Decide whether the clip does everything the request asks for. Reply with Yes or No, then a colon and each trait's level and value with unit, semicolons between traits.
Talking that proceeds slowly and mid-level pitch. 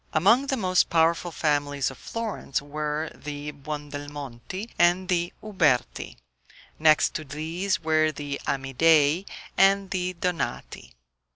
Yes: slow, 115 wpm; medium, 155 Hz